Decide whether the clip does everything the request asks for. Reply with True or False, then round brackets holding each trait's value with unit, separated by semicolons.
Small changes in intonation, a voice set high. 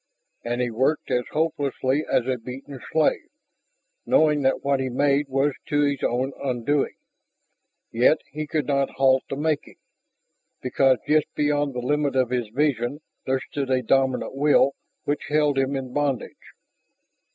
False (2.2 semitones; 135 Hz)